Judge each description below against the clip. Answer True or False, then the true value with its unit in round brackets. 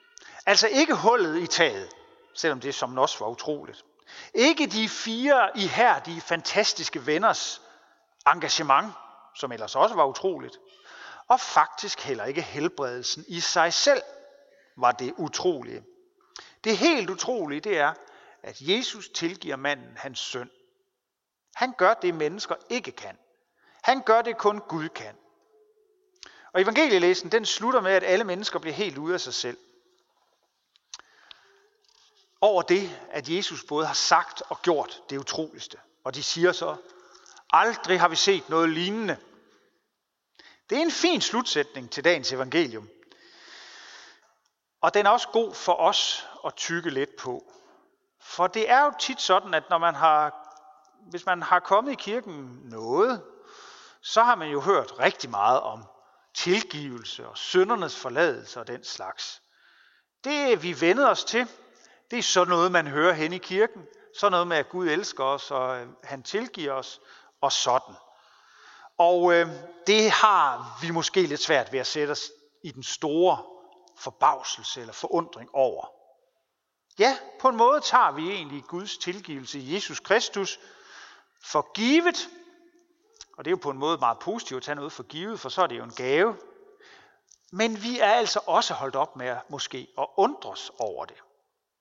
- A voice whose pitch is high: True (200 Hz)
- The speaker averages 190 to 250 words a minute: False (155 wpm)